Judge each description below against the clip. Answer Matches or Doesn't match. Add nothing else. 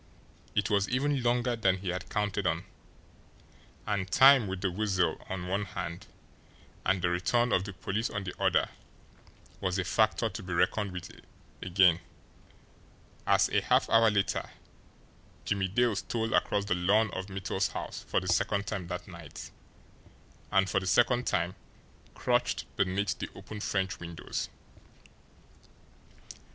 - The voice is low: Matches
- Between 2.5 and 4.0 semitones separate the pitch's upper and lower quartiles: Matches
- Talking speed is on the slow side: Doesn't match